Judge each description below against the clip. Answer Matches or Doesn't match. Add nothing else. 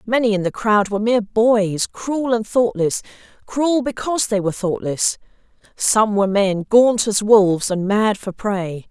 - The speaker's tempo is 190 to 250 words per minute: Doesn't match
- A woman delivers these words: Matches